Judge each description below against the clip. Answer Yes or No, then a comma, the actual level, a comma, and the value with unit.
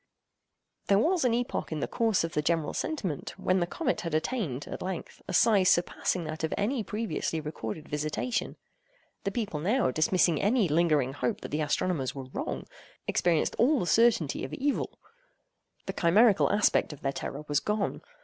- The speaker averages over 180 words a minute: No, average, 175 wpm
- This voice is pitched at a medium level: Yes, medium, 175 Hz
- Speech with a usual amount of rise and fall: No, wide, 6.4 semitones